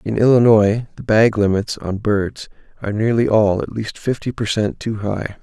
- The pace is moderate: Yes, average, 190 wpm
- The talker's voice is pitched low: Yes, low, 110 Hz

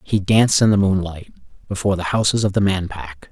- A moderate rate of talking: No, fast, 215 wpm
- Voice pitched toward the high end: No, very low, 95 Hz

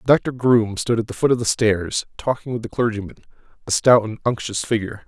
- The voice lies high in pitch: No, low, 115 Hz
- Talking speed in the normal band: No, fast, 215 wpm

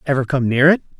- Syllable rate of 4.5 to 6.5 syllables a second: No, 6.9 syllables/s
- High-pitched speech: No, low, 135 Hz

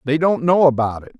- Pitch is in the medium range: Yes, medium, 145 Hz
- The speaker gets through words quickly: Yes, fast, 250 wpm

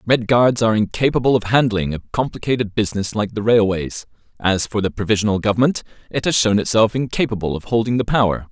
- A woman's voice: No, male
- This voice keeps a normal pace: Yes, average, 185 wpm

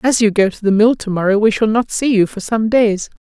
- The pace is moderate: No, fast, 280 wpm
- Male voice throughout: No, female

